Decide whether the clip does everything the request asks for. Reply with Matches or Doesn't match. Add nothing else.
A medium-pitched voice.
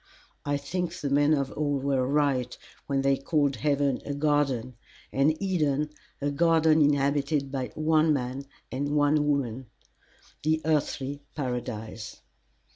Matches